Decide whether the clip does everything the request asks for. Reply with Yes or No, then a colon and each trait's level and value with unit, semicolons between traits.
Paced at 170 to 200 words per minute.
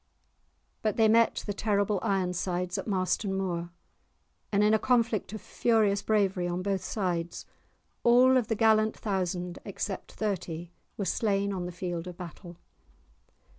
No: average, 145 wpm